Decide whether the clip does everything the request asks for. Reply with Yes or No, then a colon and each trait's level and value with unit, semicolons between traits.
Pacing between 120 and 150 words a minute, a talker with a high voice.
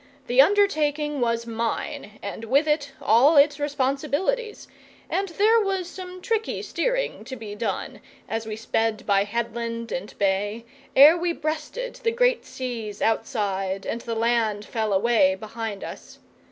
Yes: average, 145 wpm; very high, 250 Hz